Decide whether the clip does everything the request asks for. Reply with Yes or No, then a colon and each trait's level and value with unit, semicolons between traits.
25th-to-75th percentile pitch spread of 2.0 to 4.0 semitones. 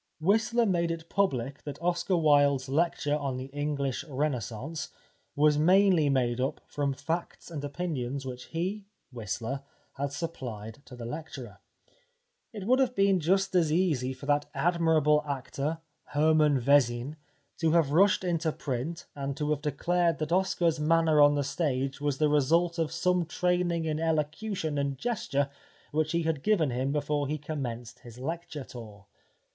Yes: average, 3.6 semitones